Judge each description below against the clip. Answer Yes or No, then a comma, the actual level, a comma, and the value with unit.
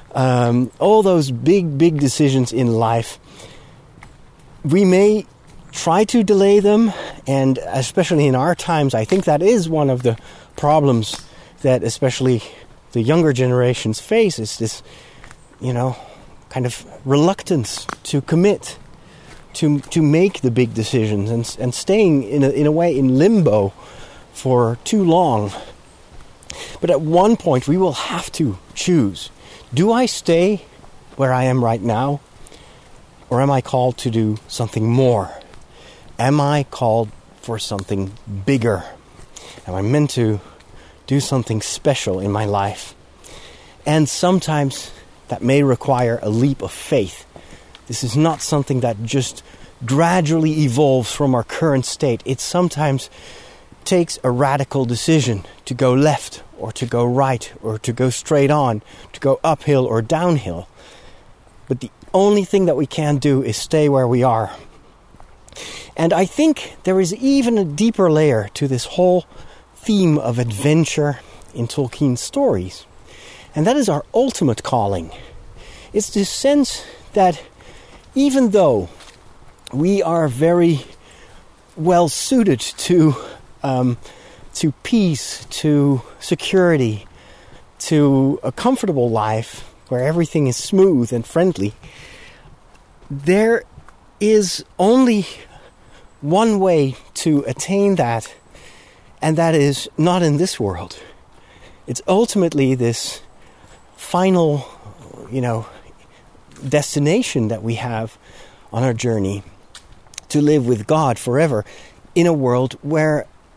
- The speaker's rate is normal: No, slow, 130 wpm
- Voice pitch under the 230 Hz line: Yes, medium, 140 Hz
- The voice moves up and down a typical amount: No, wide, 5.7 semitones